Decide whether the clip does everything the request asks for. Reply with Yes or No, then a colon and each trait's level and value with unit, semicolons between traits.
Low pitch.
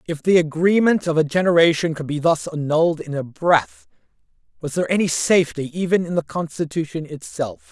No: medium, 160 Hz